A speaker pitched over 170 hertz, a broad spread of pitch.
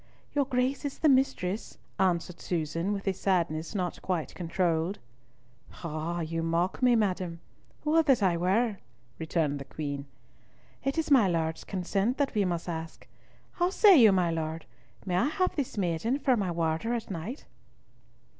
Yes: medium, 185 Hz; wide, 6.5 semitones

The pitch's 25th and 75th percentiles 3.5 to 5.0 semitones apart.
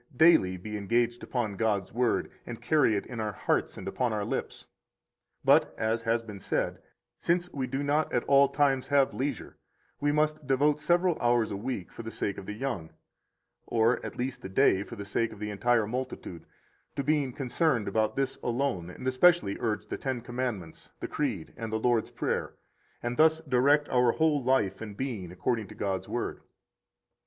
Yes: average, 4.5 semitones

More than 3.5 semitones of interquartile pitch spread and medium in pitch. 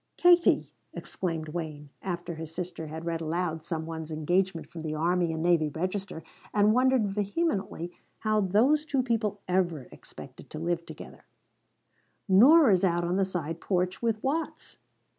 Yes: average, 4.3 semitones; medium, 180 Hz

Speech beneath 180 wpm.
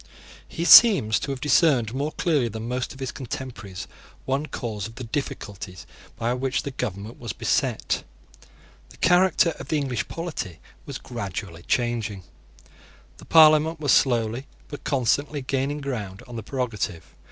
Yes: average, 150 wpm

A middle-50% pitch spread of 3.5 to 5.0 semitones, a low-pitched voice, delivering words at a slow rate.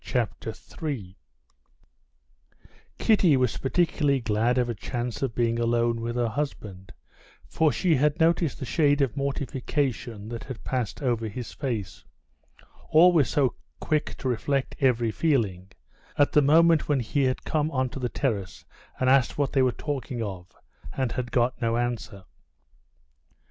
No: average, 3.8 semitones; low, 125 Hz; average, 145 wpm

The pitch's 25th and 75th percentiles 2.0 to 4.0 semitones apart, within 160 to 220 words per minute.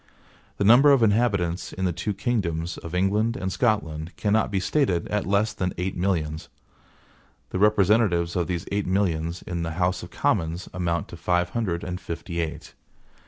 Yes: average, 3.3 semitones; average, 170 wpm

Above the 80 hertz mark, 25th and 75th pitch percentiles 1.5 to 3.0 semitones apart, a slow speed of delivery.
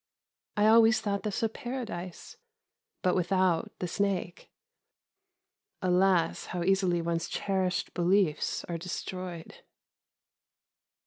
Yes: medium, 185 Hz; narrow, 2.4 semitones; slow, 100 wpm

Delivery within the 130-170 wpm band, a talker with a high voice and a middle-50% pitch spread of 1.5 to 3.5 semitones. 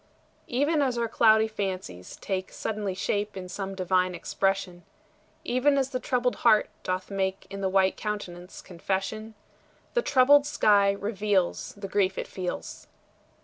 Yes: average, 145 wpm; high, 200 Hz; average, 3.2 semitones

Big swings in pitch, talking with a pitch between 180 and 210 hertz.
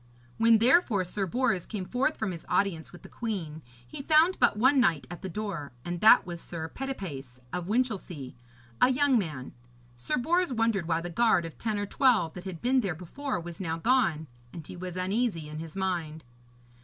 Yes: wide, 6.4 semitones; high, 190 Hz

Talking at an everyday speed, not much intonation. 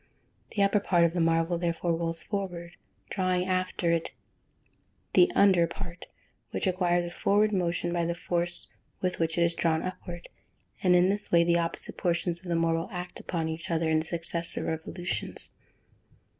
Yes: average, 170 wpm; narrow, 1.6 semitones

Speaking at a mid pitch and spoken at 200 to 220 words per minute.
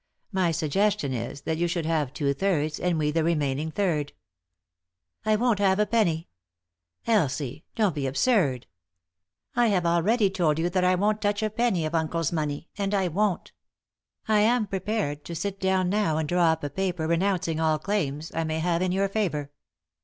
Yes: medium, 170 Hz; fast, 205 wpm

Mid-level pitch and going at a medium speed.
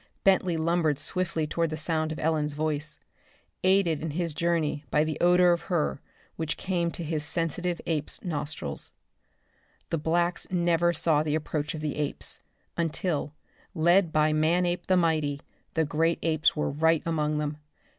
Yes: medium, 160 Hz; average, 155 wpm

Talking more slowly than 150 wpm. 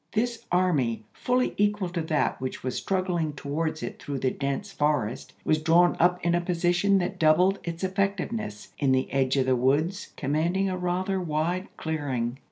No: average, 175 wpm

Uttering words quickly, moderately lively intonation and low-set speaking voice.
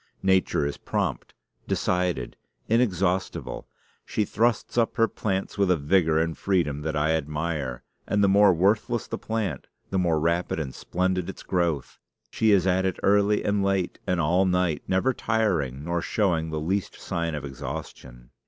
No: average, 160 wpm; average, 3.8 semitones; very low, 90 Hz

